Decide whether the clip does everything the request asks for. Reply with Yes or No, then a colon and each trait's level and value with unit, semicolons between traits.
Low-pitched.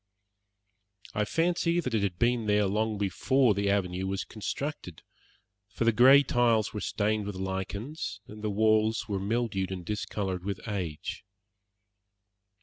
Yes: low, 105 Hz